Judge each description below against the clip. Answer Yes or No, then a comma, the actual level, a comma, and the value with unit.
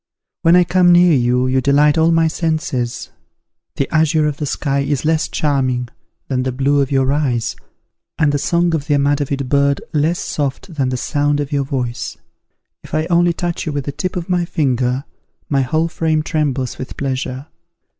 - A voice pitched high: No, medium, 145 Hz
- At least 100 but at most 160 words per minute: No, average, 185 wpm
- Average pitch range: Yes, average, 3.1 semitones